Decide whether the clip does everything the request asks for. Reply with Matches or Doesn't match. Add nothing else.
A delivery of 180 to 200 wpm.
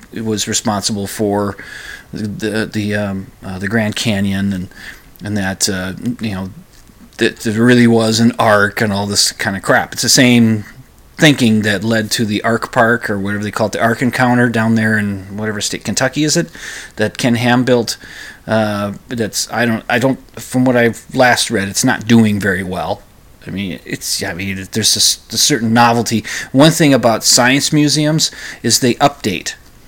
Matches